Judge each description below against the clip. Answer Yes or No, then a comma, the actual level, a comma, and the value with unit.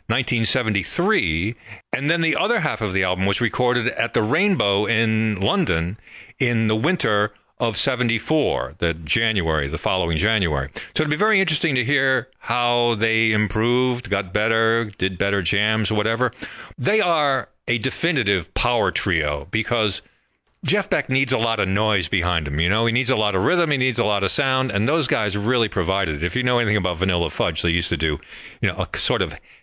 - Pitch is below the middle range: Yes, low, 110 Hz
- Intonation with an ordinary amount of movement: Yes, average, 4.5 semitones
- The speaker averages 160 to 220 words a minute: Yes, average, 190 wpm